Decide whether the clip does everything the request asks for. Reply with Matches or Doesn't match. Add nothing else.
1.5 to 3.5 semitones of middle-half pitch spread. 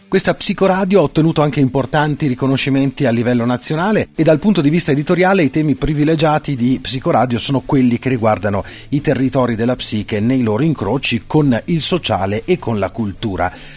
Doesn't match